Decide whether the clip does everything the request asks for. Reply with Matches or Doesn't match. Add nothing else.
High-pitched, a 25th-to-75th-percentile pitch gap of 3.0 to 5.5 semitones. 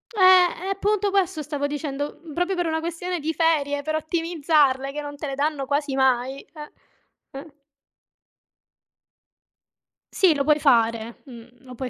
Matches